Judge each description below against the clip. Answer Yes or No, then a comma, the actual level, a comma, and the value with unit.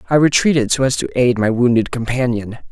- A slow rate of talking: No, average, 200 wpm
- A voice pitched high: No, low, 120 Hz